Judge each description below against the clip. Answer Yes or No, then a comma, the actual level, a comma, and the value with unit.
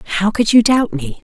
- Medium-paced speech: No, fast, 230 wpm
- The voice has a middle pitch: No, high, 205 Hz